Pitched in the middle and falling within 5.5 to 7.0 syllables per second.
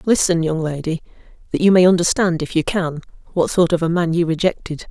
Yes: medium, 170 Hz; 5.8 syllables/s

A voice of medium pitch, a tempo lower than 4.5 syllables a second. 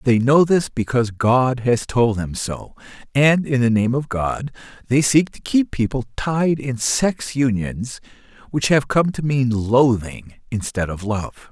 No: low, 125 Hz; 3.9 syllables/s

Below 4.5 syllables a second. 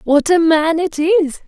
Yes: 3.7 syllables/s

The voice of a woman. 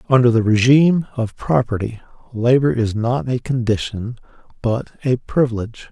No: male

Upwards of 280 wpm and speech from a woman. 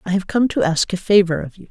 Yes: fast, 315 wpm; female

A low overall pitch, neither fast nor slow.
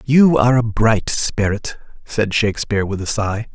Yes: low, 110 Hz; average, 170 wpm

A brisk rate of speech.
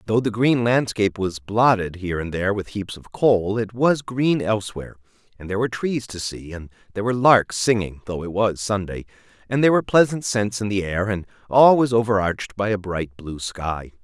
Yes: fast, 215 wpm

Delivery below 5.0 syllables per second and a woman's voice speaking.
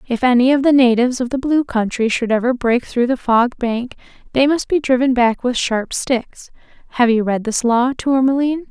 No: 5.1 syllables/s; female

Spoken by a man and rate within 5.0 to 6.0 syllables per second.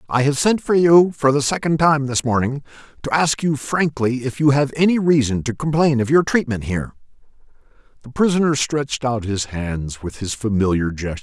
Yes: male; 5.3 syllables/s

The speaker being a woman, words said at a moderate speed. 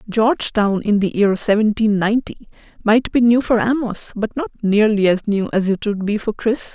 Yes: female; average, 195 wpm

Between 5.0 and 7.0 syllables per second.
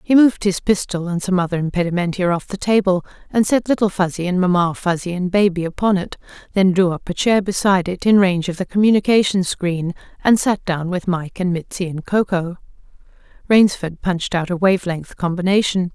Yes: 5.7 syllables/s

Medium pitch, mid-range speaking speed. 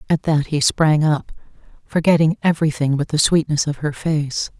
Yes: medium, 155 Hz; average, 170 wpm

